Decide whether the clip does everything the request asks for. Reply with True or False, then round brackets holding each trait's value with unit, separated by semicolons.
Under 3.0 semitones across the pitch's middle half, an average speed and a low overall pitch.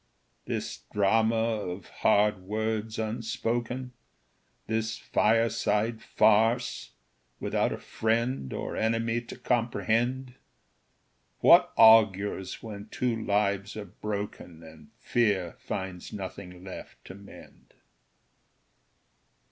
False (2.4 semitones; 90 wpm; 110 Hz)